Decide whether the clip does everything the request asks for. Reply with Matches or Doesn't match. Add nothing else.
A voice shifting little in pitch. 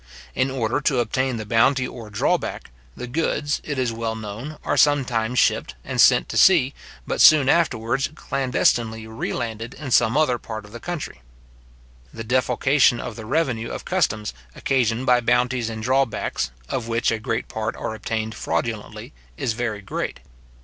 Doesn't match